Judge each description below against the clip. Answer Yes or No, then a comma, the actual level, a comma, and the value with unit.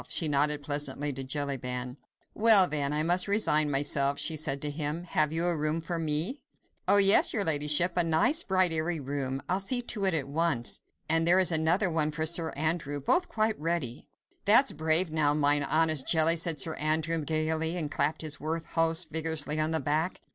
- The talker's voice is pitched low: No, medium, 160 Hz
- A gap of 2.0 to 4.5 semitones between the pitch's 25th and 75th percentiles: Yes, narrow, 2.6 semitones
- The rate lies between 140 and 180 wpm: No, average, 190 wpm